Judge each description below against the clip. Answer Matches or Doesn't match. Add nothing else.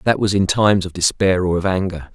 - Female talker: Doesn't match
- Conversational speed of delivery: Doesn't match